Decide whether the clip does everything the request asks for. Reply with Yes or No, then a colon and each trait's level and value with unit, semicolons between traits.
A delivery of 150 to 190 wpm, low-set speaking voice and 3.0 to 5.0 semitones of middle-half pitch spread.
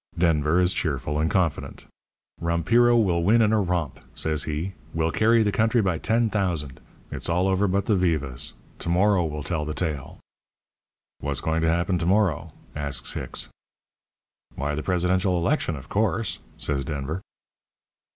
Yes: average, 155 wpm; very low, 85 Hz; average, 4.4 semitones